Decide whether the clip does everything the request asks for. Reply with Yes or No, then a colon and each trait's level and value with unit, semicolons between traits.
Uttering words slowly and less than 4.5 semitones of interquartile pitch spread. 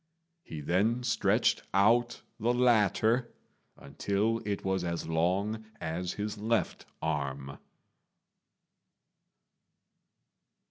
No: slow, 85 wpm; average, 5.1 semitones